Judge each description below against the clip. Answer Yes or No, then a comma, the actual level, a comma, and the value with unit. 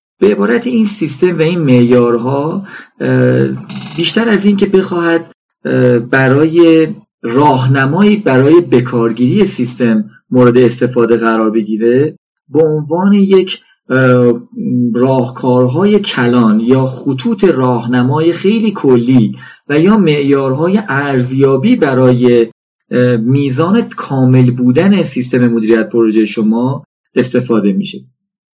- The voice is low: Yes, low, 130 Hz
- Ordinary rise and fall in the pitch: No, wide, 5.9 semitones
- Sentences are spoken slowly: Yes, slow, 95 wpm